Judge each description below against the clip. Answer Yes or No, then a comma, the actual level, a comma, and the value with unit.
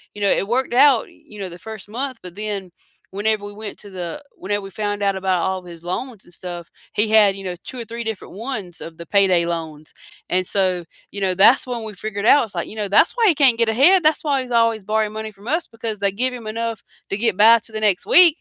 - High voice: Yes, high, 210 Hz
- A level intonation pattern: No, average, 3.5 semitones